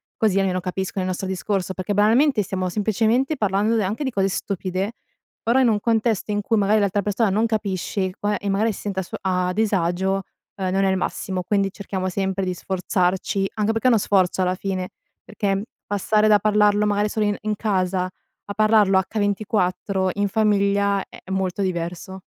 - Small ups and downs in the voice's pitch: Yes, narrow, 2.0 semitones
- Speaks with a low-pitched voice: No, high, 200 Hz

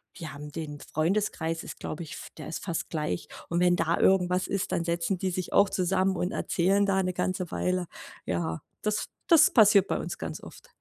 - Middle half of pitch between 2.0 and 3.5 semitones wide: Yes, average, 2.8 semitones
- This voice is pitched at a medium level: Yes, medium, 180 Hz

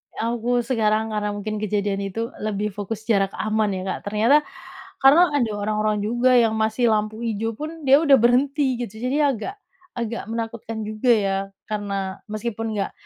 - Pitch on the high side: Yes, high, 220 Hz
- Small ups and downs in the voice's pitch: Yes, narrow, 2.3 semitones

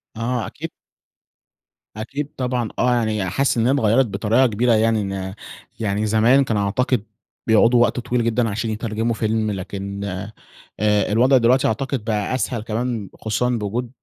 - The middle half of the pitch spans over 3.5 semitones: No, narrow, 2.6 semitones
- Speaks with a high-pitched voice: No, low, 115 Hz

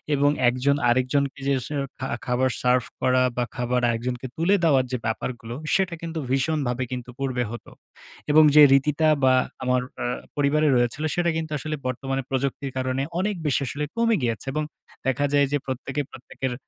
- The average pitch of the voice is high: No, low, 135 Hz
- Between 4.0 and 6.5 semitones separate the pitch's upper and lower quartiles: No, average, 2.9 semitones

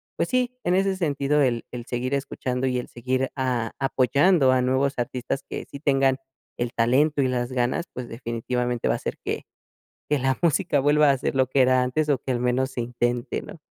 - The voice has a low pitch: Yes, low, 130 Hz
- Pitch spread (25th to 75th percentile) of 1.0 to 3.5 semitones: Yes, narrow, 2.4 semitones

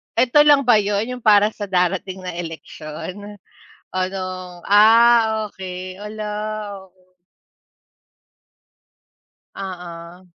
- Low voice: No, high, 195 Hz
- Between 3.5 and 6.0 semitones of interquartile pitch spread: No, average, 3.0 semitones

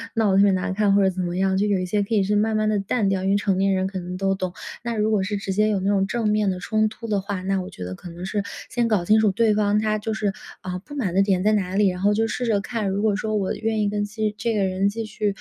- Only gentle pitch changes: Yes, narrow, 2.0 semitones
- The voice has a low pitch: No, high, 205 Hz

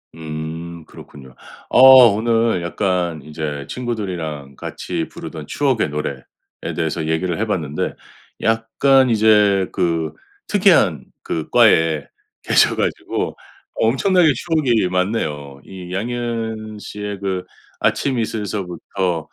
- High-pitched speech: No, very low, 95 Hz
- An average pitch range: No, wide, 5.8 semitones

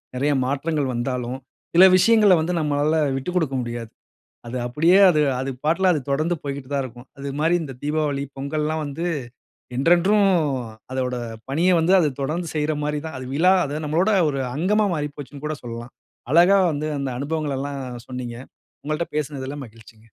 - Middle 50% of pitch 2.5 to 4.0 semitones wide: Yes, average, 3.4 semitones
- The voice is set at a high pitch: No, medium, 150 Hz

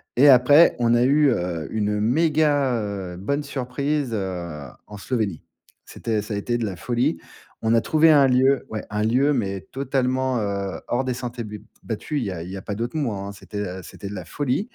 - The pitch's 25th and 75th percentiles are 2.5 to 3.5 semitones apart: No, average, 4.9 semitones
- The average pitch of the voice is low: Yes, low, 120 Hz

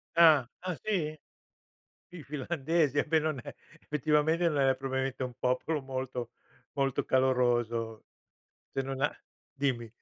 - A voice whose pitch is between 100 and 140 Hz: Yes, low, 135 Hz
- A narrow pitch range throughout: No, average, 3.1 semitones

